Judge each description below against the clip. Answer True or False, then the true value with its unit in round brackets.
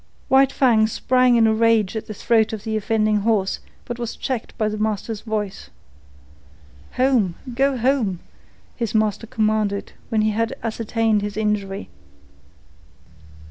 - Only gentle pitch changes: True (1.8 semitones)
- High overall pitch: True (220 Hz)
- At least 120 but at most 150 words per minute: True (140 wpm)